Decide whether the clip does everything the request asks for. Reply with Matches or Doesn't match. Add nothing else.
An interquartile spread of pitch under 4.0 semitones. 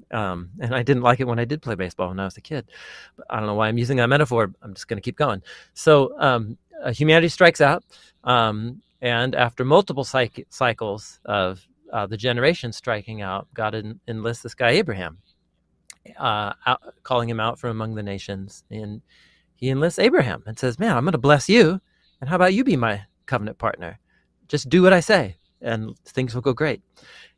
Doesn't match